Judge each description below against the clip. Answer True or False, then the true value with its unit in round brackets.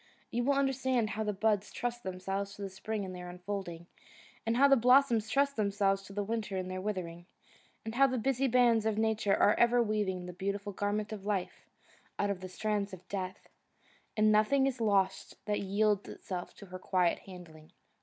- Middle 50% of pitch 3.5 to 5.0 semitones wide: False (3.1 semitones)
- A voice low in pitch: False (205 Hz)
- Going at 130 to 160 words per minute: False (195 wpm)